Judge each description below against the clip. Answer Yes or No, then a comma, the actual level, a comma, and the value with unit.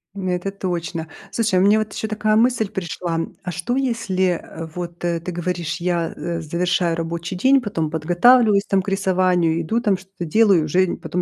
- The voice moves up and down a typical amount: Yes, average, 3.2 semitones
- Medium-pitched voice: Yes, medium, 180 Hz